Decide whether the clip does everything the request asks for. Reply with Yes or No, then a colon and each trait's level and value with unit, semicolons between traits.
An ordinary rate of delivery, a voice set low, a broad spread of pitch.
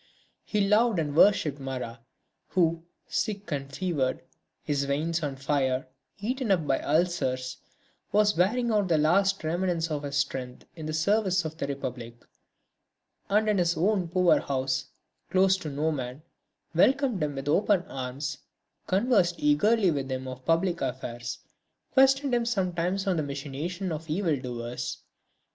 No: average, 150 wpm; medium, 160 Hz; wide, 5.8 semitones